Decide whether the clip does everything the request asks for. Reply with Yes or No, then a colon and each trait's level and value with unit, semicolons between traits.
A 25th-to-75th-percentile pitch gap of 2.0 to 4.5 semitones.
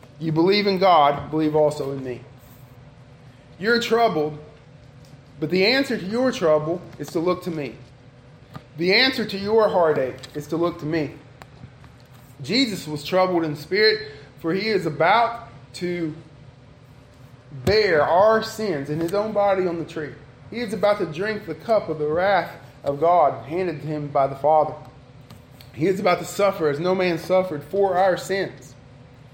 No: wide, 5.4 semitones